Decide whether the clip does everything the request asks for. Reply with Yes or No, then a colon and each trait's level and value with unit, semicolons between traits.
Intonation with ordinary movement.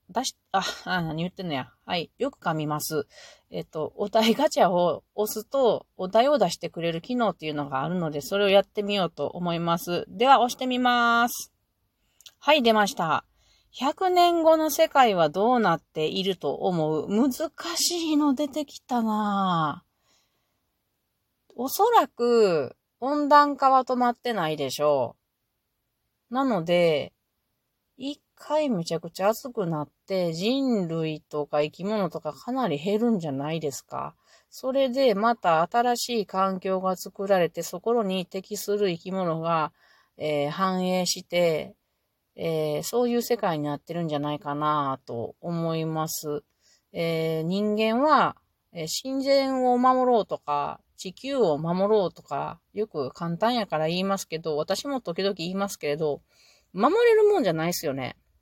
No: wide, 7.2 semitones